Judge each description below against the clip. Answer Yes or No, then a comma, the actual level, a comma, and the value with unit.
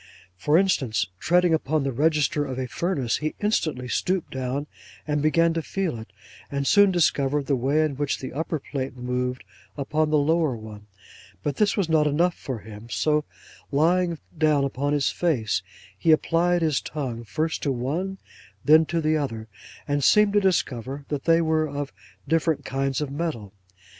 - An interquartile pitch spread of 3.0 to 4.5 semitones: Yes, average, 3.8 semitones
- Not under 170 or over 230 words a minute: Yes, average, 175 wpm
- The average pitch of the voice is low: No, medium, 150 Hz